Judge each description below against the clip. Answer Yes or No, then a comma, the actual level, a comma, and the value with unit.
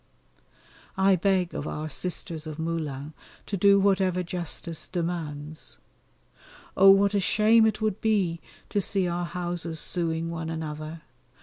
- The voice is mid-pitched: Yes, medium, 175 Hz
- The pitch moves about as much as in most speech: Yes, average, 3.2 semitones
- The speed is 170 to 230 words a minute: No, slow, 135 wpm